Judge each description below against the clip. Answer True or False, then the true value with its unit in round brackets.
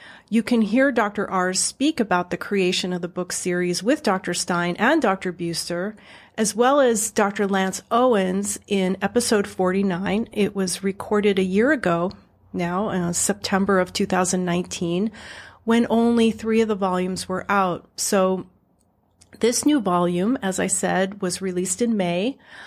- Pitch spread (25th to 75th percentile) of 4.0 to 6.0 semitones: False (3.4 semitones)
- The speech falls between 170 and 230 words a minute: False (155 wpm)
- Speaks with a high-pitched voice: True (195 Hz)